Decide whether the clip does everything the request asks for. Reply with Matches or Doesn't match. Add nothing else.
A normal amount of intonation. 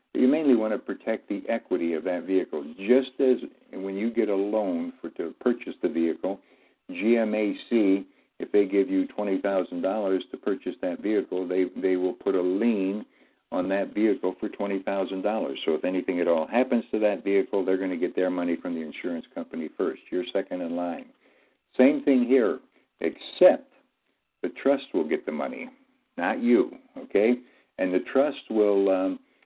Matches